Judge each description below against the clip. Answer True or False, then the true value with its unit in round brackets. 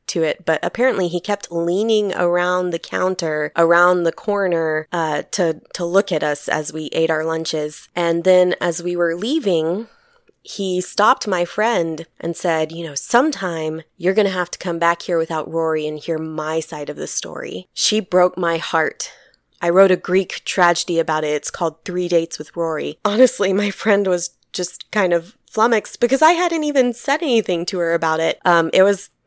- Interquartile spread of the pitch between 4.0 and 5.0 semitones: False (3.3 semitones)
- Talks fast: False (190 wpm)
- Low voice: False (175 Hz)